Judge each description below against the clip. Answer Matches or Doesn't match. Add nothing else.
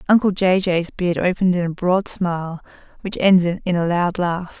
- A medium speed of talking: Matches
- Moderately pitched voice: Matches